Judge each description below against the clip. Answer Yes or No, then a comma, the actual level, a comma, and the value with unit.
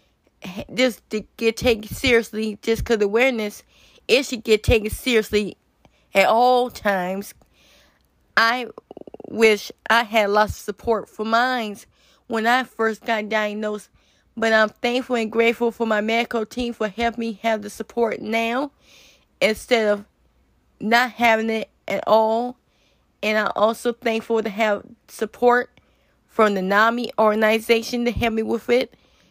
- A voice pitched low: No, high, 225 Hz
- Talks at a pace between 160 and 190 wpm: No, average, 145 wpm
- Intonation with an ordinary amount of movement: No, narrow, 1.9 semitones